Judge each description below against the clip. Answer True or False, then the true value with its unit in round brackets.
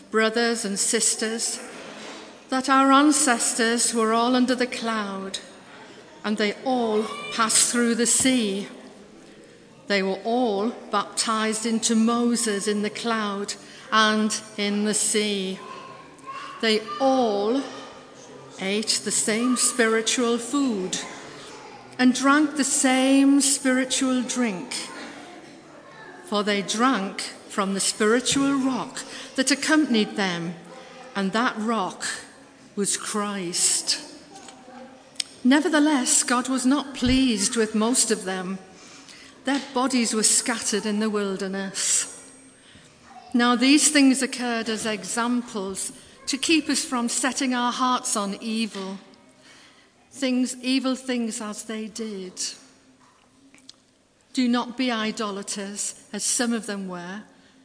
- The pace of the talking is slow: True (110 wpm)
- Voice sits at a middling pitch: False (235 Hz)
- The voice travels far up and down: False (3.7 semitones)